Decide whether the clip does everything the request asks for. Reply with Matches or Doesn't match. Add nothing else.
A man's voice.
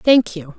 Doesn't match